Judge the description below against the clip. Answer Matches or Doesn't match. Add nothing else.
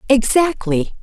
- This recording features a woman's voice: Matches